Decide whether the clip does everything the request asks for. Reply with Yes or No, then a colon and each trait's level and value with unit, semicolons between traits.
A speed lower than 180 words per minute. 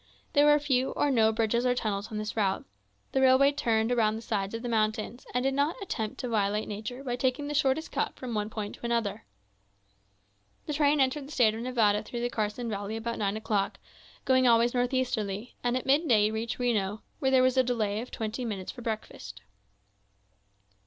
No: average, 200 wpm